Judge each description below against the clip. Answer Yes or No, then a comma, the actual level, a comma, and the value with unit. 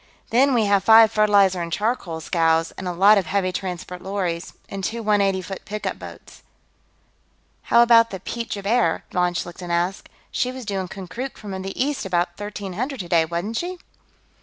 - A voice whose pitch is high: Yes, high, 195 Hz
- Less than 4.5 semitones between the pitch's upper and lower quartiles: Yes, average, 3.9 semitones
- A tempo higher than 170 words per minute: Yes, average, 180 wpm